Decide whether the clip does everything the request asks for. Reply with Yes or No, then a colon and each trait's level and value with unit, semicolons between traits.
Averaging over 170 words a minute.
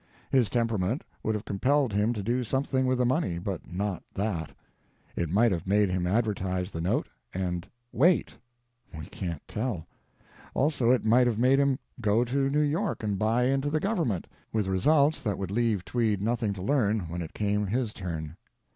Yes: average, 180 wpm